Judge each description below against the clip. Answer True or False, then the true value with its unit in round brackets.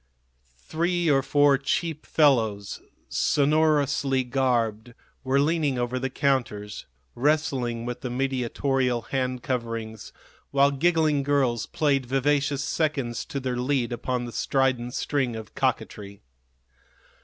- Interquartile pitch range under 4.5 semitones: True (2.9 semitones)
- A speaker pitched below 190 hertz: True (135 Hz)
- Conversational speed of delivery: False (115 wpm)